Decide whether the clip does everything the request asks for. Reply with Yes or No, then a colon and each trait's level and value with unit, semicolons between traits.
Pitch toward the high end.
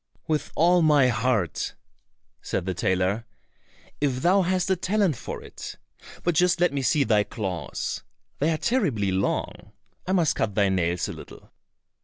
No: medium, 140 Hz